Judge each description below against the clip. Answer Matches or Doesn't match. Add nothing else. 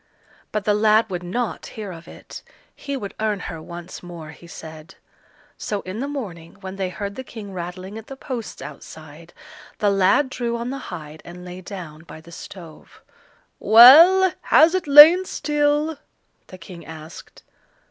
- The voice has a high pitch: Matches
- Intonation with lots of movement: Matches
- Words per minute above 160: Matches